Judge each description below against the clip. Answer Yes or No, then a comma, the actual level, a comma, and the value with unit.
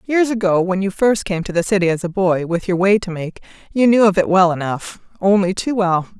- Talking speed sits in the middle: No, fast, 250 wpm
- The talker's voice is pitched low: No, high, 190 Hz